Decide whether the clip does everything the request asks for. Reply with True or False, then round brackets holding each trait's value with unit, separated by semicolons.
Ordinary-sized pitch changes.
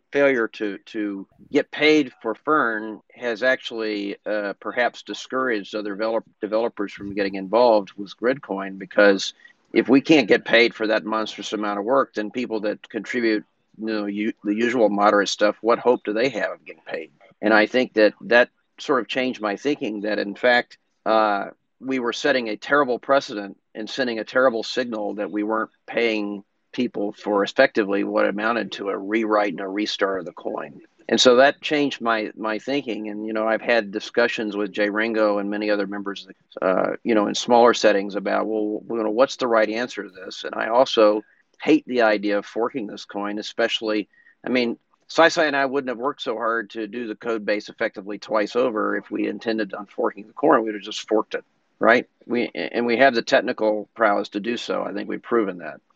False (2.3 semitones)